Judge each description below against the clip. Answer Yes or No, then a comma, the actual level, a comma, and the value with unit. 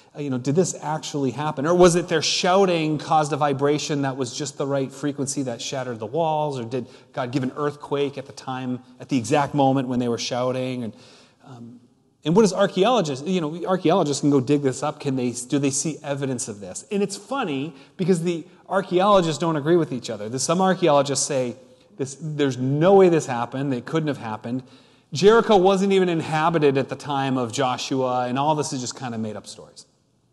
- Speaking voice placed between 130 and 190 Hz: Yes, medium, 140 Hz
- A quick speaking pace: Yes, fast, 210 wpm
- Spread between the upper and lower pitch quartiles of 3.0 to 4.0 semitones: Yes, average, 3.7 semitones